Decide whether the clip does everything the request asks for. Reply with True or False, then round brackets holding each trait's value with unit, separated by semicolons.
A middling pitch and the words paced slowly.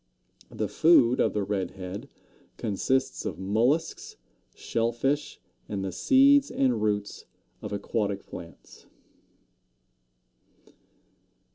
False (115 Hz; 100 wpm)